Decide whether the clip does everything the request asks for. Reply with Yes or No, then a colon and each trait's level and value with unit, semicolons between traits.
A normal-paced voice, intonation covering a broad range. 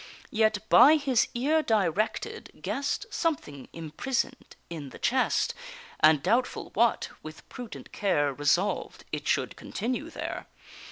No: slow, 120 wpm; wide, 8.5 semitones